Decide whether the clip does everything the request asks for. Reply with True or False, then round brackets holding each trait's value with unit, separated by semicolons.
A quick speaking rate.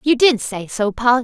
True (245 wpm)